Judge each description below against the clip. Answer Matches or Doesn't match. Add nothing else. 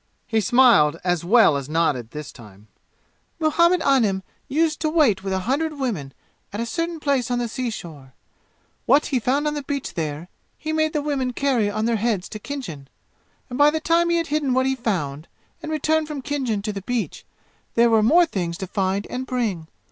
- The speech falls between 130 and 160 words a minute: Doesn't match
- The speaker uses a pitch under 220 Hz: Doesn't match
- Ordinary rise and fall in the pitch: Doesn't match